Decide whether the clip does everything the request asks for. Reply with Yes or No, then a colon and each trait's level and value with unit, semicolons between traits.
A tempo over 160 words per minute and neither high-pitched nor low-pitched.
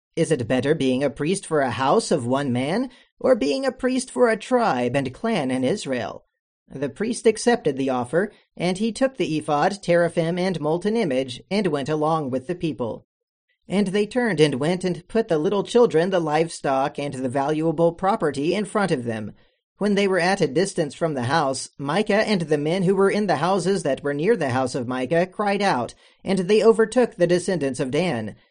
Yes: fast, 205 wpm; medium, 175 Hz